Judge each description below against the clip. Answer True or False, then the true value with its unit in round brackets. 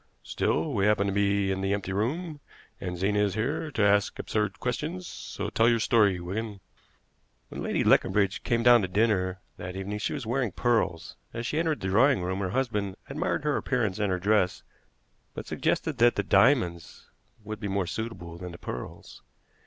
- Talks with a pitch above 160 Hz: False (105 Hz)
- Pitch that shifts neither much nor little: True (3.7 semitones)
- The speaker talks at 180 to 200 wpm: True (185 wpm)